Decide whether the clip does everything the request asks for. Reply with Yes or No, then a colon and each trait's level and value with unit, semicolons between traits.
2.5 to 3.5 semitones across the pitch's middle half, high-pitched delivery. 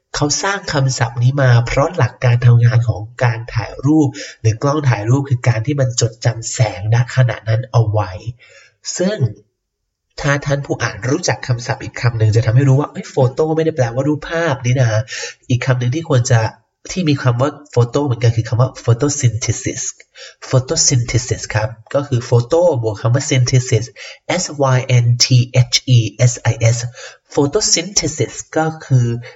No: average, 3.2 semitones; low, 125 Hz